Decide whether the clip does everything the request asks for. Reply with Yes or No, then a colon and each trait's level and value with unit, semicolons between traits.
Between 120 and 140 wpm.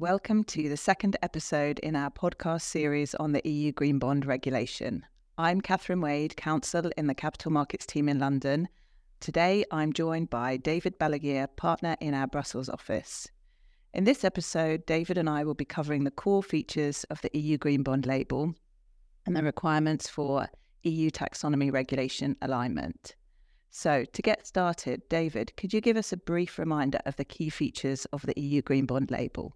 No: average, 175 wpm